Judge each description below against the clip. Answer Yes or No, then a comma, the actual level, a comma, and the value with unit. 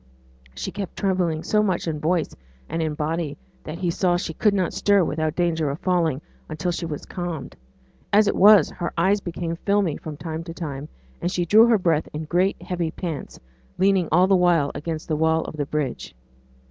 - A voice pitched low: No, medium, 170 Hz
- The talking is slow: No, average, 200 wpm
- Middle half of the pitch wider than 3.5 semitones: No, average, 2.8 semitones